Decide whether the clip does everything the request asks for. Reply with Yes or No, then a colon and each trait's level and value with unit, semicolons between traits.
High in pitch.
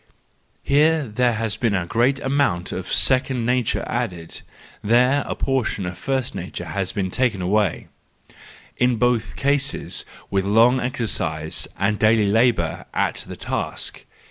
No: low, 115 Hz